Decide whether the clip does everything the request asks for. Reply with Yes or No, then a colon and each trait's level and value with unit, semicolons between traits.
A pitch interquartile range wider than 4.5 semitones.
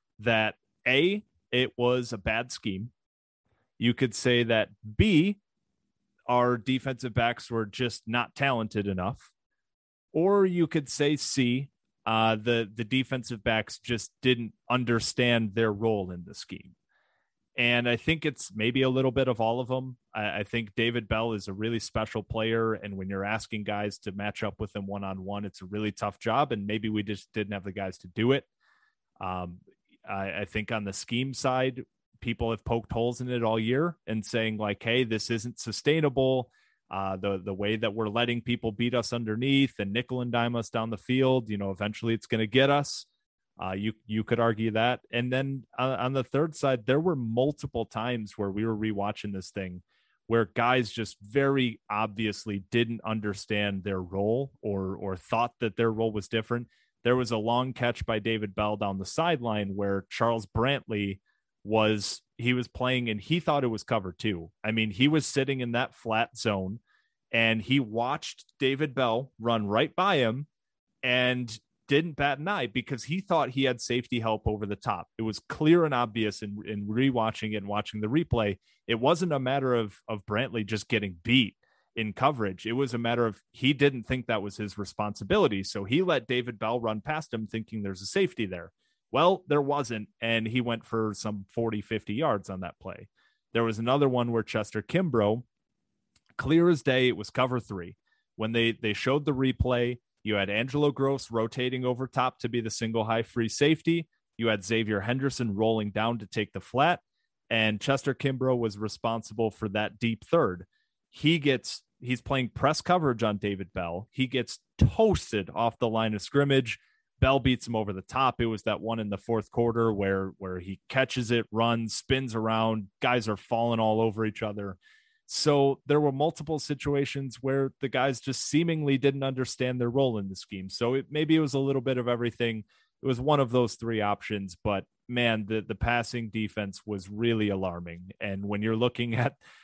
No: average, 3.3 semitones